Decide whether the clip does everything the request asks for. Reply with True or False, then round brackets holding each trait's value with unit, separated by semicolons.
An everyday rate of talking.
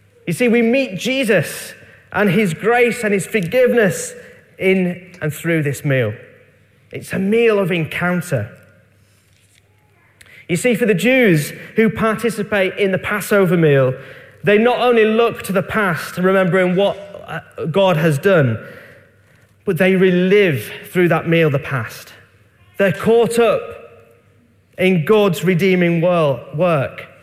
False (130 wpm)